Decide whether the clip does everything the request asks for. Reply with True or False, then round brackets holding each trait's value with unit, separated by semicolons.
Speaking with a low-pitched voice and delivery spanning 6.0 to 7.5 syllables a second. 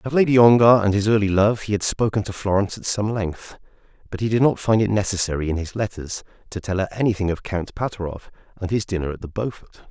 True (100 Hz; 6.4 syllables/s)